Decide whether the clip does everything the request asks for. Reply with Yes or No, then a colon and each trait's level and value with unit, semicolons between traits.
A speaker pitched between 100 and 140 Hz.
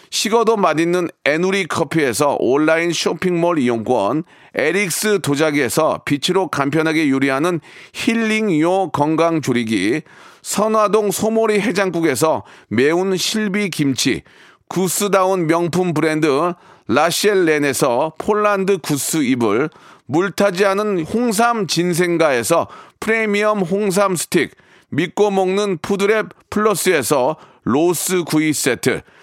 No: medium, 185 Hz